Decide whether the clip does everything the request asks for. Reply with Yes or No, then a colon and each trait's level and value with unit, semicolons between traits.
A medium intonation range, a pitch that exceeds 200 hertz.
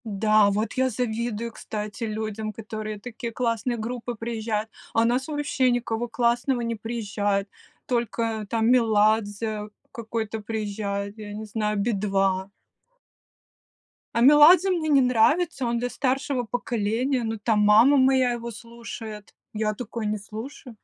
No: narrow, 2.3 semitones; high, 225 Hz